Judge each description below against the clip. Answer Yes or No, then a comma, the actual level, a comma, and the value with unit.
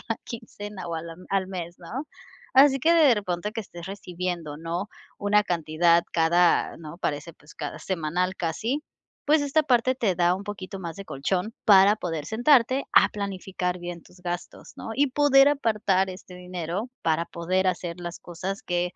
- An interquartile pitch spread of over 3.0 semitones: Yes, average, 3.9 semitones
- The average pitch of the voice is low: No, medium, 185 Hz